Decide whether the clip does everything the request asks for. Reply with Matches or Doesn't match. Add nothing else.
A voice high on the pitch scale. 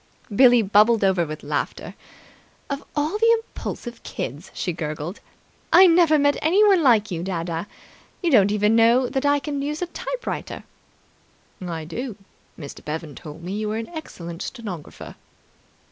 Matches